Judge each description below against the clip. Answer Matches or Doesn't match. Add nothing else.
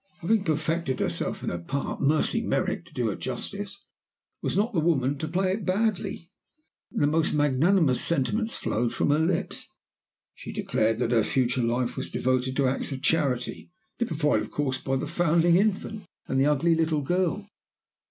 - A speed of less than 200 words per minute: Matches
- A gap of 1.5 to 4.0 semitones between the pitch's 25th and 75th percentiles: Doesn't match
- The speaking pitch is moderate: Matches